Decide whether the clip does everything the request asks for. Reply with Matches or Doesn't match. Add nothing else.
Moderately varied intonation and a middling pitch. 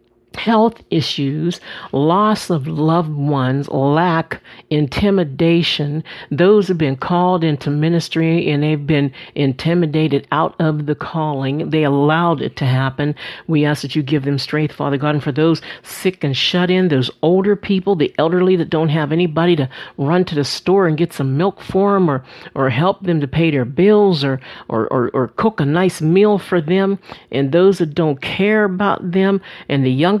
Matches